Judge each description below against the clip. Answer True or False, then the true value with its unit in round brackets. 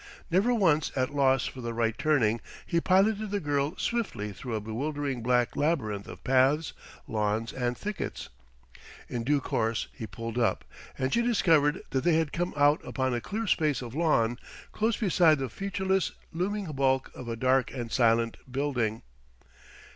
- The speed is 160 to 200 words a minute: True (165 wpm)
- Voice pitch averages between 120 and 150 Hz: True (135 Hz)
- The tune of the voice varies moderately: False (6.0 semitones)